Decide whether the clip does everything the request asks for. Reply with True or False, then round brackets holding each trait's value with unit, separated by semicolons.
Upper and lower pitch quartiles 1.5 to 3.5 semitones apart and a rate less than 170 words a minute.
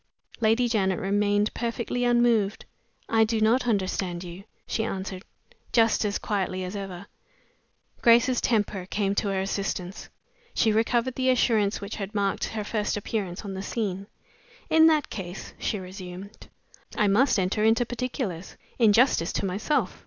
True (3.1 semitones; 150 wpm)